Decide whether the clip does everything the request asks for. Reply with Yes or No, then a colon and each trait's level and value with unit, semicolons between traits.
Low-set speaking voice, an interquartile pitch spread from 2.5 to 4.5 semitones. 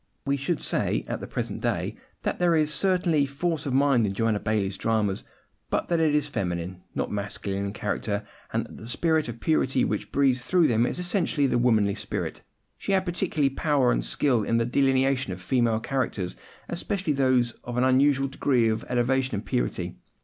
No: low, 130 Hz; average, 5.0 semitones